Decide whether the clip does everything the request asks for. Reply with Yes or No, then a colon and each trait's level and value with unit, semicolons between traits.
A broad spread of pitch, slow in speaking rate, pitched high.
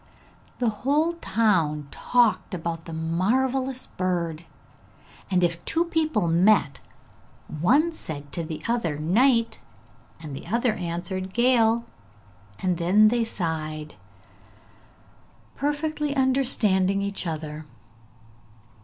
Yes: wide, 6.9 semitones; slow, 100 wpm; high, 195 Hz